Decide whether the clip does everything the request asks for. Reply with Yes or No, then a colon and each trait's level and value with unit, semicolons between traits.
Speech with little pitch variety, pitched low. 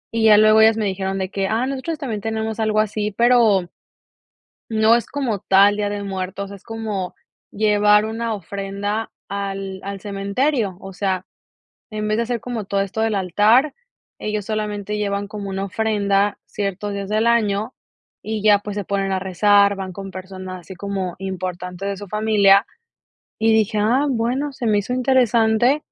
No: narrow, 2.1 semitones; high, 205 Hz